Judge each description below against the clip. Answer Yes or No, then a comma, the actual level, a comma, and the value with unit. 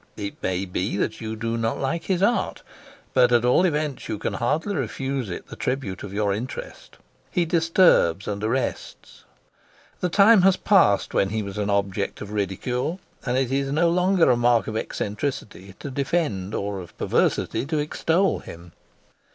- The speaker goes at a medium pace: Yes, average, 175 wpm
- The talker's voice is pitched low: Yes, low, 120 Hz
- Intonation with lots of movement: Yes, wide, 7.8 semitones